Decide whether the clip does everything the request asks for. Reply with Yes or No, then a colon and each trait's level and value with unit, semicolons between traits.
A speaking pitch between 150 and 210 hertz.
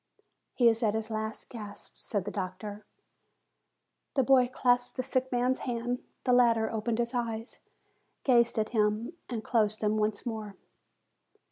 No: high, 230 Hz